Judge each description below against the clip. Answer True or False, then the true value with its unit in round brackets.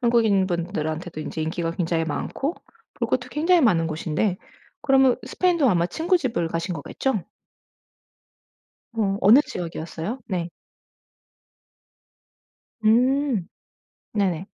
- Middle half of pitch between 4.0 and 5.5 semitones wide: False (7.5 semitones)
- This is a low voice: False (195 Hz)